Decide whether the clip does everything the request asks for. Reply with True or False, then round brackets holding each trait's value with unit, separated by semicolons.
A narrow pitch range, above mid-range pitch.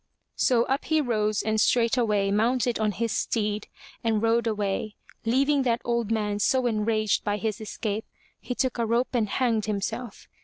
True (2.3 semitones; 225 Hz)